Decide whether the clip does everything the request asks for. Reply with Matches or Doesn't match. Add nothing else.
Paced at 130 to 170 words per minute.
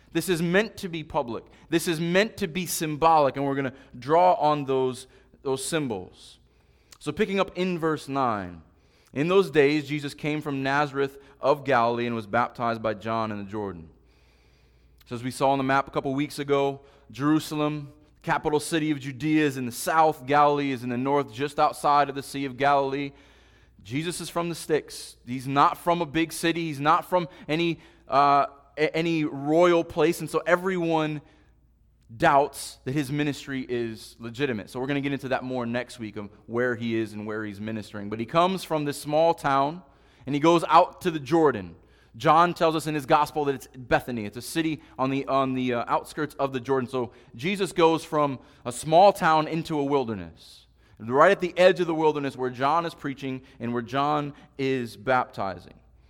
Doesn't match